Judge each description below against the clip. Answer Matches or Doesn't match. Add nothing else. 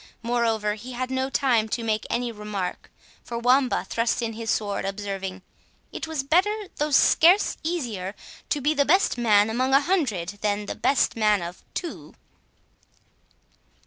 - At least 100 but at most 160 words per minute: Matches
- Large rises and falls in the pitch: Doesn't match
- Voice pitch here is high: Matches